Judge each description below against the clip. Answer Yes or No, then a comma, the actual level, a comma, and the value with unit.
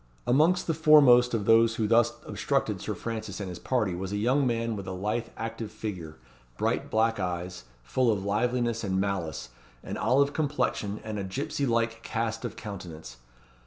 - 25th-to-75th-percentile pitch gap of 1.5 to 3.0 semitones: No, average, 3.8 semitones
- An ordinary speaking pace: Yes, average, 175 wpm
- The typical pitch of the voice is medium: No, low, 110 Hz